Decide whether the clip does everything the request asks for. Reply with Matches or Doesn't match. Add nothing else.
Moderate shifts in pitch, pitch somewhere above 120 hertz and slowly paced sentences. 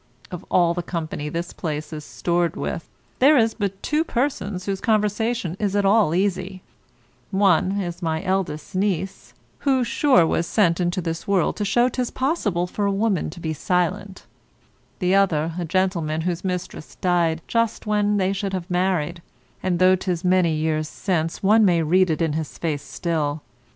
Doesn't match